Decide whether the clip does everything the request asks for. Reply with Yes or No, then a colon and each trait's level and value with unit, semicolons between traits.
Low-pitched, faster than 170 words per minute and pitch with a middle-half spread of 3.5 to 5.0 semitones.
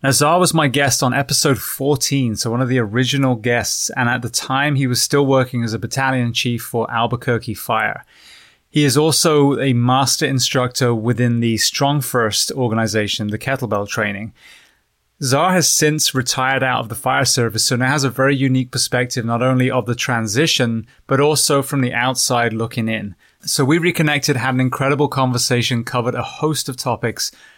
No: low, 130 Hz; average, 180 wpm; average, 2.8 semitones